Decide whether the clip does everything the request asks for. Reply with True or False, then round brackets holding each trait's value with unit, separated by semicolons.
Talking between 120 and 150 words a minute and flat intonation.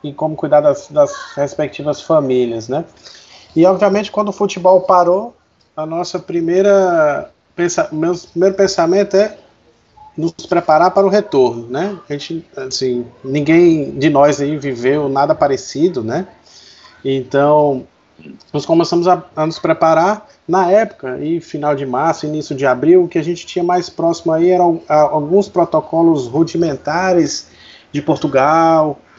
False (140 wpm; 3.8 semitones)